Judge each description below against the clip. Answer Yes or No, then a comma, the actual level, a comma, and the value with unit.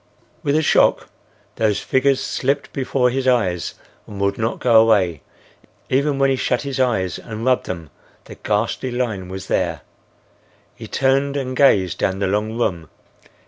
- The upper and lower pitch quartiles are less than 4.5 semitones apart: No, average, 5.2 semitones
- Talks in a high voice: No, low, 120 Hz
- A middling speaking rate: Yes, average, 160 wpm